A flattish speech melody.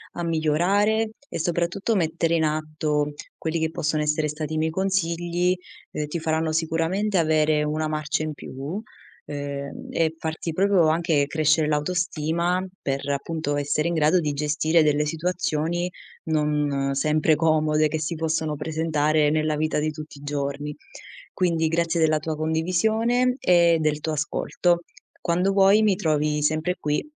Yes: narrow, 2.1 semitones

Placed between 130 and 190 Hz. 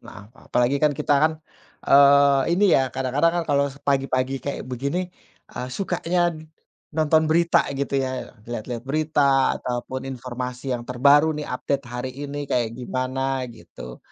Yes: low, 135 Hz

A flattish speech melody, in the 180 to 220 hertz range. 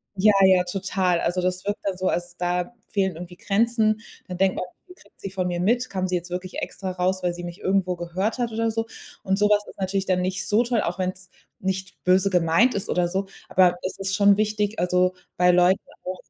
Yes: narrow, 2.0 semitones; medium, 185 Hz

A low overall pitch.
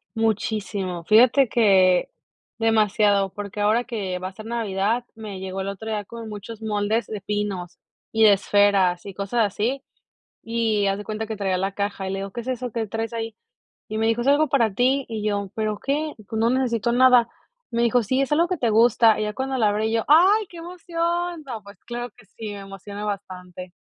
No: high, 220 Hz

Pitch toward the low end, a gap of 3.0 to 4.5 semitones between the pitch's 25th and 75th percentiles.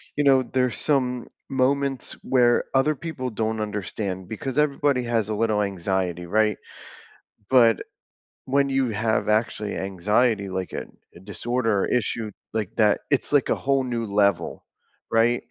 Yes: low, 115 Hz; average, 4.0 semitones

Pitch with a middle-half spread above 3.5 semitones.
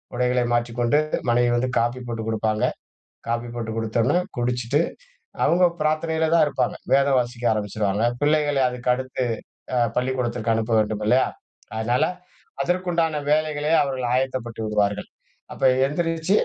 Yes: average, 4.2 semitones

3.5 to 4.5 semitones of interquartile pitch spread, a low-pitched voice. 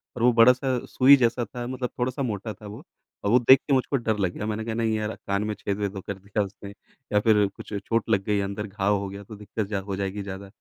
No: average, 3.0 semitones; low, 105 Hz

